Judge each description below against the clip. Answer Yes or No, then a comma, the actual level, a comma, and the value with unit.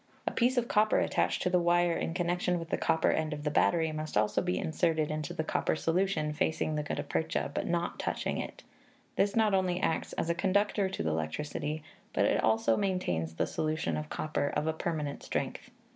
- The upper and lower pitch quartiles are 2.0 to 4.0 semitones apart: Yes, average, 3.1 semitones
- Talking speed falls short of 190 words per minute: No, fast, 205 wpm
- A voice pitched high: No, medium, 160 Hz